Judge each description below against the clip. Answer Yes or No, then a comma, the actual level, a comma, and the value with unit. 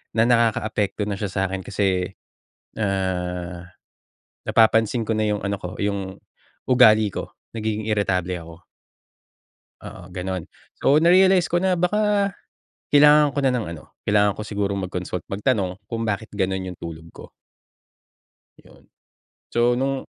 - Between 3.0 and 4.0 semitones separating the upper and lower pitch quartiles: No, average, 4.5 semitones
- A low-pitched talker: Yes, low, 105 Hz